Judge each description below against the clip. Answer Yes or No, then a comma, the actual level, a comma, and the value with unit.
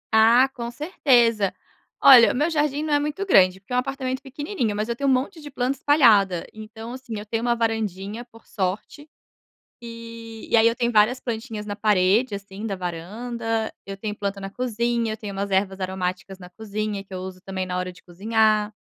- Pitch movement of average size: Yes, average, 3.9 semitones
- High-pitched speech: Yes, high, 225 Hz